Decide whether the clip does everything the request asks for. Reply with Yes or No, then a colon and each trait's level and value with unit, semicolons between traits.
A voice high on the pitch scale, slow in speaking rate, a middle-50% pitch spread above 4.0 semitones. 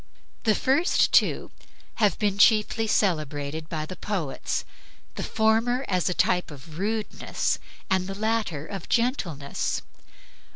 Yes: high, 195 Hz; slow, 120 wpm; wide, 5.5 semitones